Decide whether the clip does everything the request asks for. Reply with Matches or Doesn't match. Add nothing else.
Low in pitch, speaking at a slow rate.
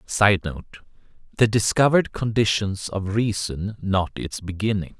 Matches